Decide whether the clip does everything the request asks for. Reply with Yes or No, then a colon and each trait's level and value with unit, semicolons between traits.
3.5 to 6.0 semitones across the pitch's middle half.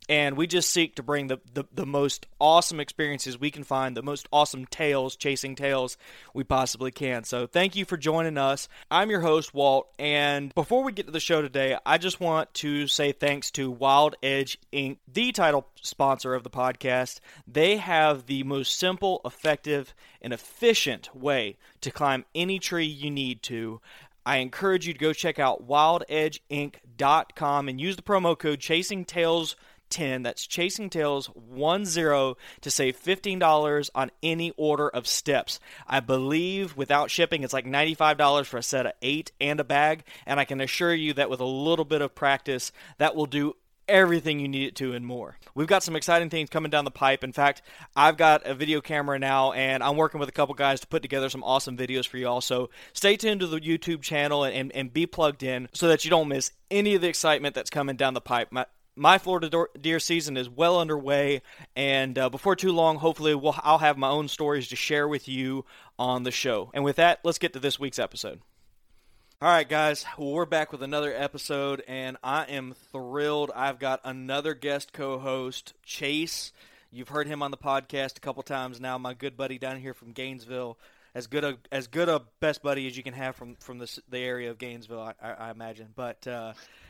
No: average, 3.1 semitones